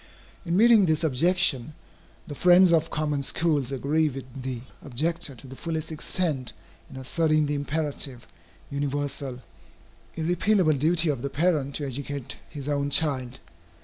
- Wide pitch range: No, average, 3.2 semitones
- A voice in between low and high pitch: Yes, medium, 145 Hz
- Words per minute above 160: No, average, 140 wpm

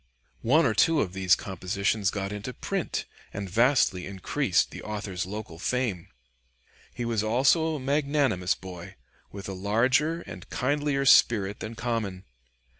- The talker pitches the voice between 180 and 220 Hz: No, low, 110 Hz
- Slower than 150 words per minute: Yes, average, 140 wpm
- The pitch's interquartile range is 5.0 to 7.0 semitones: Yes, wide, 5.4 semitones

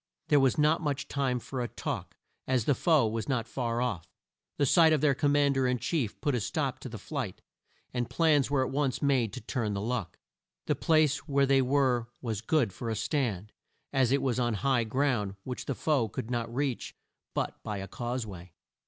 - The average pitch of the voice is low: Yes, low, 130 Hz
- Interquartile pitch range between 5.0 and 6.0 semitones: No, average, 3.6 semitones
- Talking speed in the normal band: No, fast, 215 wpm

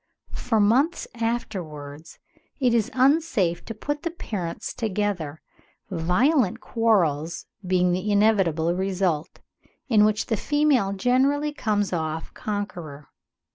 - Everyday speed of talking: No, slow, 110 wpm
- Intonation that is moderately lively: No, wide, 5.8 semitones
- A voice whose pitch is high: Yes, high, 205 Hz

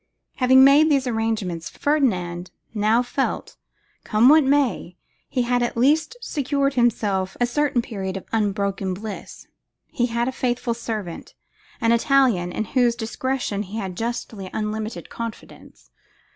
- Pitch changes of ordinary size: Yes, average, 4.1 semitones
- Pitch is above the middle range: Yes, high, 235 Hz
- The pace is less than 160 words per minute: Yes, average, 145 wpm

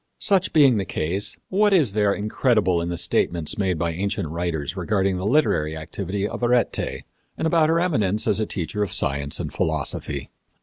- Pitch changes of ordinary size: No, wide, 6.2 semitones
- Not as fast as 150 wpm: No, average, 180 wpm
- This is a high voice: No, low, 100 Hz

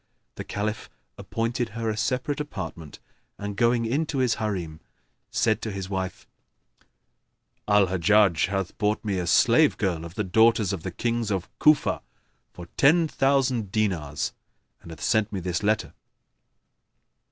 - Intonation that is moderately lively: Yes, average, 3.8 semitones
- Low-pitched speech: Yes, low, 105 Hz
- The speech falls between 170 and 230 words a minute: No, average, 145 wpm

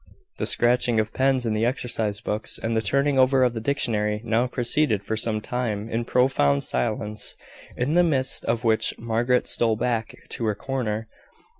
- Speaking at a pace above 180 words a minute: No, average, 175 wpm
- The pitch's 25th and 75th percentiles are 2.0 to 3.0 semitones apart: Yes, average, 2.7 semitones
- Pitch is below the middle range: Yes, low, 115 Hz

